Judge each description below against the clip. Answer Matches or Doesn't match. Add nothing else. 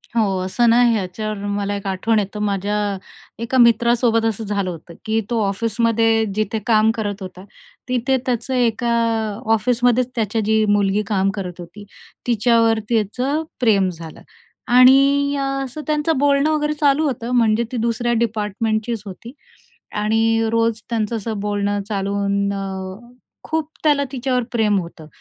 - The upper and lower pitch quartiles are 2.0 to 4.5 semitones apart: Matches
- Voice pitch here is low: Doesn't match